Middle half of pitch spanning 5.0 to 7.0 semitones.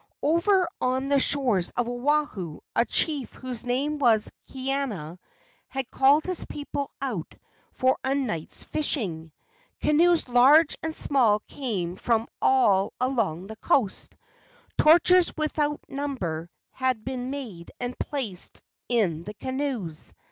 Yes: average, 5.3 semitones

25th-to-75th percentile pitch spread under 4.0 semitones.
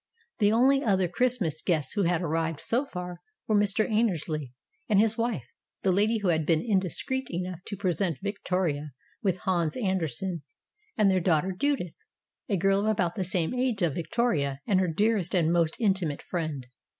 No: average, 4.3 semitones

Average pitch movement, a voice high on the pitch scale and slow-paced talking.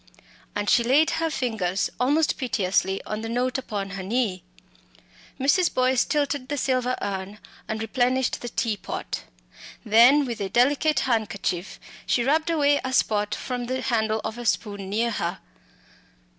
No: average, 4.1 semitones; high, 240 Hz; average, 155 wpm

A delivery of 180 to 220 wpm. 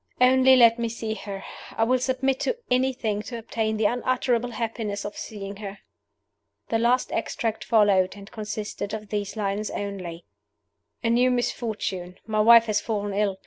No: average, 160 wpm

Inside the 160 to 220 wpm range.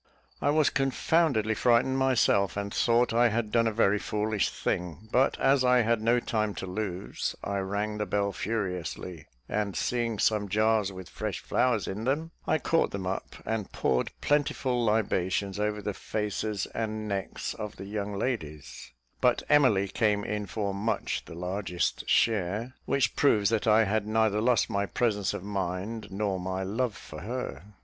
Yes: average, 170 wpm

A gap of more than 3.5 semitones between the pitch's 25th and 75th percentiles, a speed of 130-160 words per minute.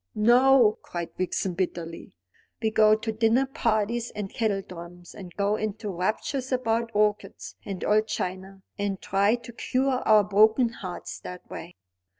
No: average, 3.2 semitones; average, 145 wpm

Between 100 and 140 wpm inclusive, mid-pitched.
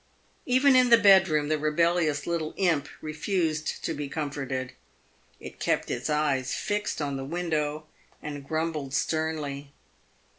Yes: slow, 135 wpm; medium, 155 Hz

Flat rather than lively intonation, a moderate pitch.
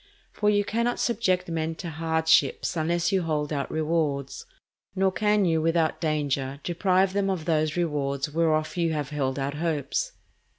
No: average, 3.4 semitones; medium, 160 Hz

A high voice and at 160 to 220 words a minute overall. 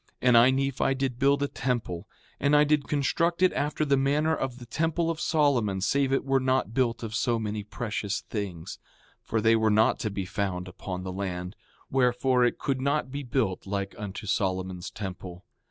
No: low, 120 Hz; average, 195 wpm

